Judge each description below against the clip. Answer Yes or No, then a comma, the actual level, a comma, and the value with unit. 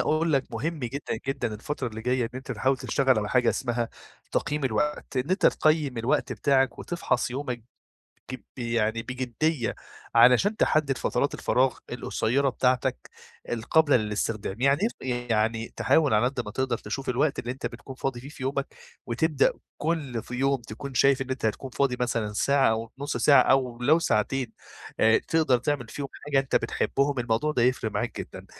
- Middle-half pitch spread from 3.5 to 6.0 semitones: No, average, 3.0 semitones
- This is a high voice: No, low, 130 Hz